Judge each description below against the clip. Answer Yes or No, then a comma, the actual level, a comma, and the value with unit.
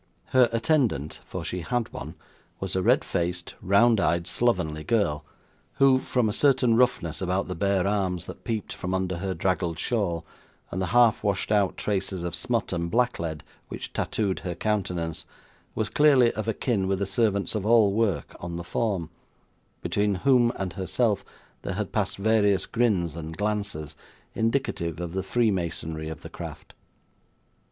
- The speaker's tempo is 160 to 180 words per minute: Yes, average, 165 wpm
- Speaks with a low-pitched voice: Yes, low, 100 Hz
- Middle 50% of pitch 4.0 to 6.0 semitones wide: Yes, average, 4.6 semitones